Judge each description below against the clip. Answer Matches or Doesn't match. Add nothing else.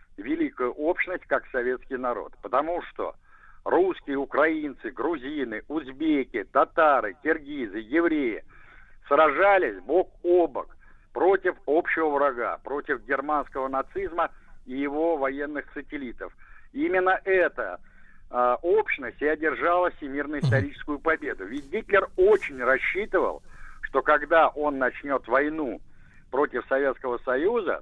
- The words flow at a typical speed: Doesn't match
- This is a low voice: Doesn't match